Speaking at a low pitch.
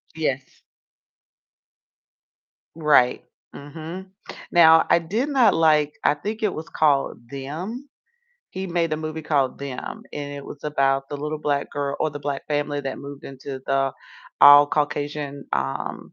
No: medium, 145 Hz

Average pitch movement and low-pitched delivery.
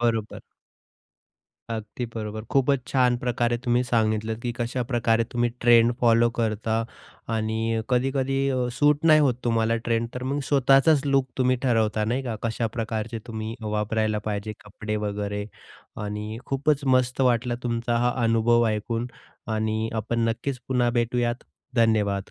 No: narrow, 2.2 semitones; low, 115 Hz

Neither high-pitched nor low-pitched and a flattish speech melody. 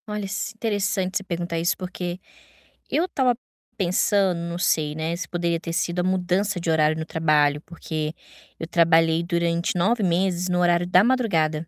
Yes: medium, 175 Hz; narrow, 2.3 semitones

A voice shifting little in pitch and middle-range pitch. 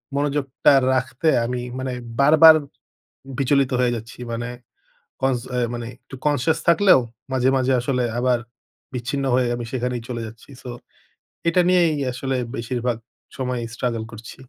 No: narrow, 2.3 semitones; low, 125 Hz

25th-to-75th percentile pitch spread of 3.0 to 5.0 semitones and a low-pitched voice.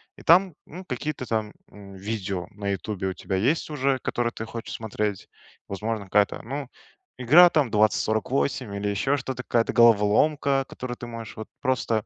Yes: average, 4.4 semitones; low, 115 Hz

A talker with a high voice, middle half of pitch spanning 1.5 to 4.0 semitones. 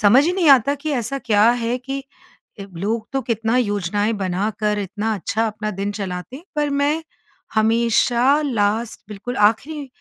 No: high, 225 Hz; average, 4.6 semitones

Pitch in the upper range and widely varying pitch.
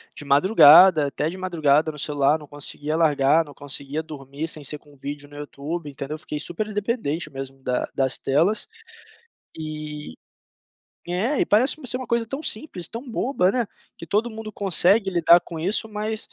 No: medium, 160 Hz; wide, 6.1 semitones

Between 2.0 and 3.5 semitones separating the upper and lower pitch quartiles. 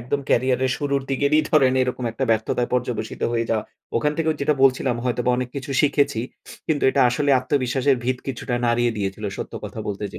Yes: average, 2.9 semitones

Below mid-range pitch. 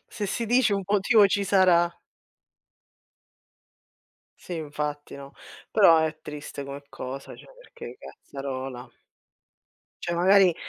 No: medium, 170 Hz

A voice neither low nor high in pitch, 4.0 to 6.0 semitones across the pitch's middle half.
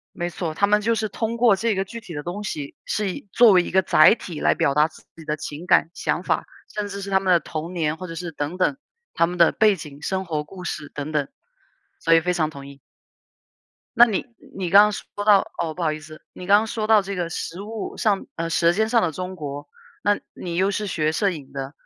Yes: medium, 180 Hz; average, 4.5 semitones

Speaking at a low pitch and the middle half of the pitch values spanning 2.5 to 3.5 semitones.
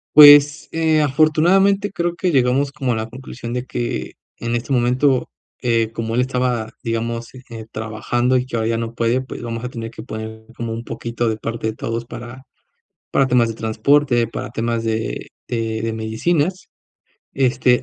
Yes: low, 120 Hz; average, 2.8 semitones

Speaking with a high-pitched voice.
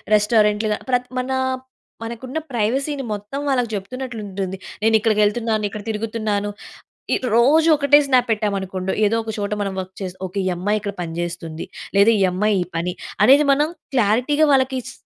Yes: high, 215 Hz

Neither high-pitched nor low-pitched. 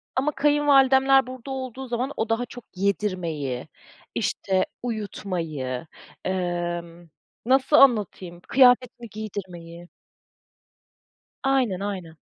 No: high, 210 Hz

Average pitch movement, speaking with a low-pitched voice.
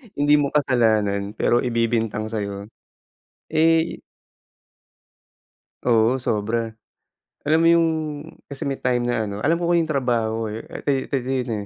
Yes: average, 4.3 semitones; low, 120 Hz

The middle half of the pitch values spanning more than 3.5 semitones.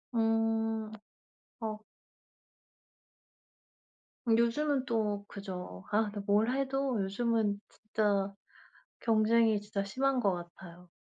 No: narrow, 2.4 semitones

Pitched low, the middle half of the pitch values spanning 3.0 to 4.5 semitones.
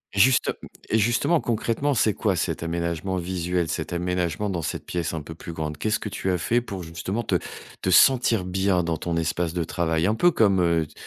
Yes: very low, 90 Hz; average, 4.0 semitones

